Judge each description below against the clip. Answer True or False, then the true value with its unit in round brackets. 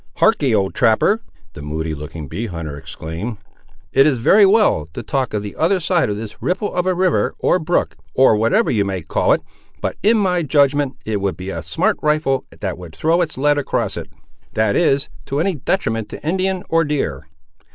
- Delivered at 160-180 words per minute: False (195 wpm)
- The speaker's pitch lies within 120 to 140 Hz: True (135 Hz)